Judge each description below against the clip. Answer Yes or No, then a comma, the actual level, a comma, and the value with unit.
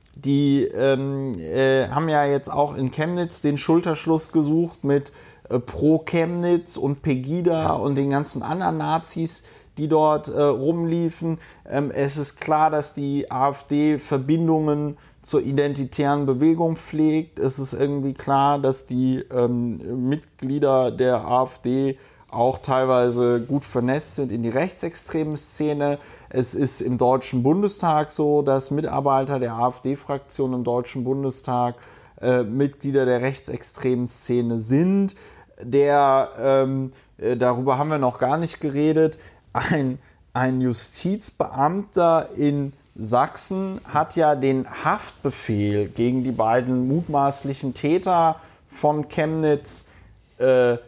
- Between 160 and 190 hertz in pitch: No, medium, 140 Hz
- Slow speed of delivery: Yes, slow, 120 wpm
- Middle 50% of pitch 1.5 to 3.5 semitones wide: Yes, average, 3.1 semitones